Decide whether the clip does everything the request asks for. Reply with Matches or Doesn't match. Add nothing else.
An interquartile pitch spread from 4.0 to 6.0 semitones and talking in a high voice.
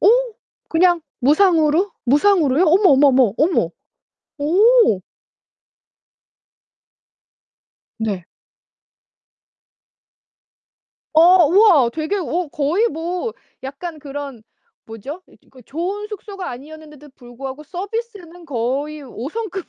Matches